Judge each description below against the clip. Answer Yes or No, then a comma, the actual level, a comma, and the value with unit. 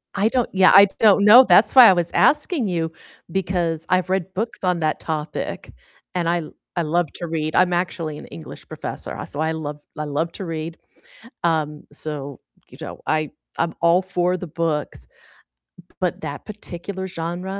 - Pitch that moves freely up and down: No, average, 3.2 semitones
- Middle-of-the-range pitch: Yes, medium, 170 Hz